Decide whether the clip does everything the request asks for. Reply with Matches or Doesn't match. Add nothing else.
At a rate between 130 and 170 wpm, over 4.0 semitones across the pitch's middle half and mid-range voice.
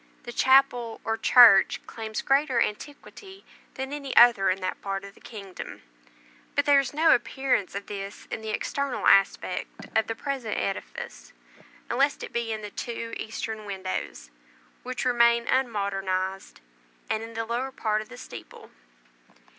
Doesn't match